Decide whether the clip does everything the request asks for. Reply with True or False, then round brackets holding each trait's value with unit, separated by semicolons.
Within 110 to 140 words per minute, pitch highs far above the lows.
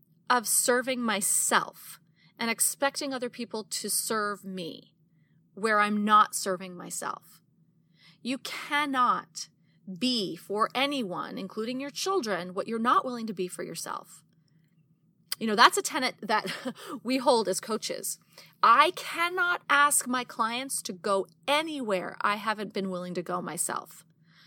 True (135 wpm; 6.2 semitones)